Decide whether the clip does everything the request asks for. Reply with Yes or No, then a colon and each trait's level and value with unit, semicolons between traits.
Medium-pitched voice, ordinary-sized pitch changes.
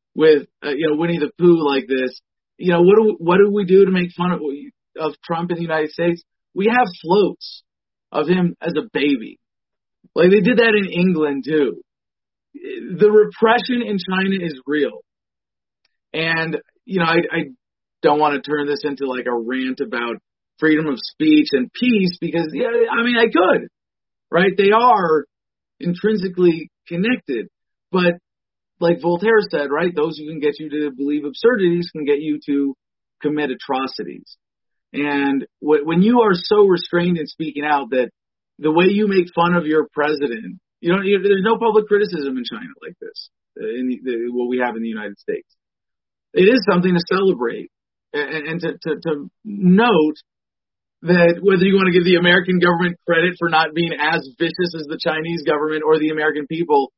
Yes: medium, 170 Hz; average, 4.6 semitones